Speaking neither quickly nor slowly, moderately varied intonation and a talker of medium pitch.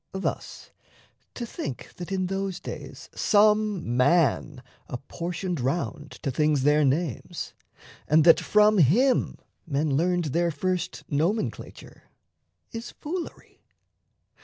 No: slow, 110 wpm; average, 4.9 semitones; medium, 170 Hz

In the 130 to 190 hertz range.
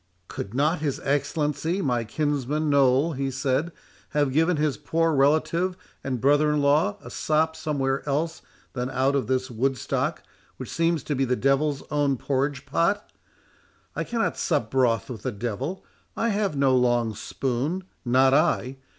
Yes: medium, 140 Hz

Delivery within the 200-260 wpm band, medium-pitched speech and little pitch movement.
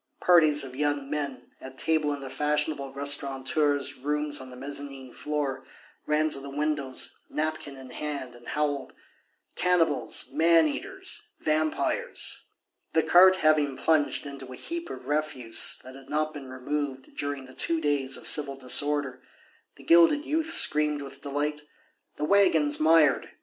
No: average, 150 wpm; medium, 145 Hz; narrow, 2.2 semitones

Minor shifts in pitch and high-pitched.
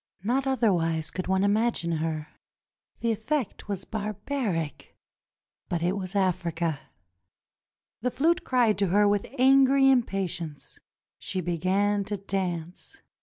No: average, 5.0 semitones; high, 200 Hz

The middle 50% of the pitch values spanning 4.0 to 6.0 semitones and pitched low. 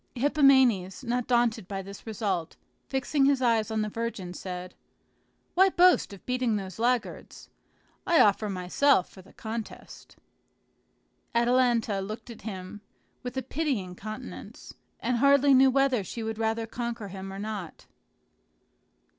No: average, 4.3 semitones; high, 225 Hz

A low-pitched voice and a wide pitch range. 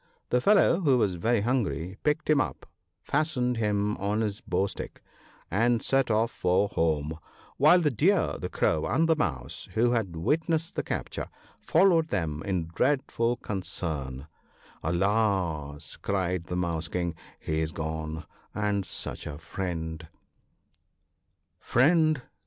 Yes: low, 100 Hz; wide, 7.3 semitones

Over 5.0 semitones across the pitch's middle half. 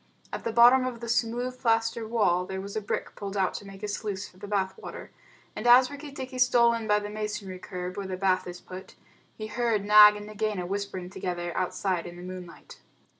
No: average, 3.7 semitones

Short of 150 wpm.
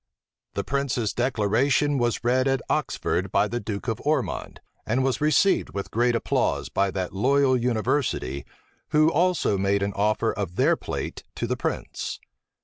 No: average, 155 wpm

